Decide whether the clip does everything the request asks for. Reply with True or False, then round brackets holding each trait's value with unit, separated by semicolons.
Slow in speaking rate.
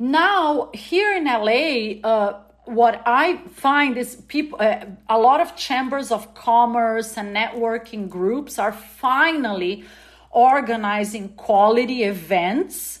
True (115 wpm)